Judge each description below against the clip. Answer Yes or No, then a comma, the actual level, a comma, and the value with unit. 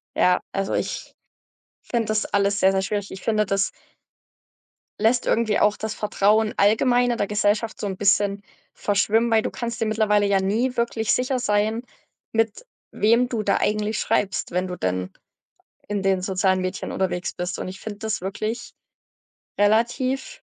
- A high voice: Yes, high, 210 Hz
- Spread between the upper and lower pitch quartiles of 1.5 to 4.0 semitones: Yes, narrow, 2.4 semitones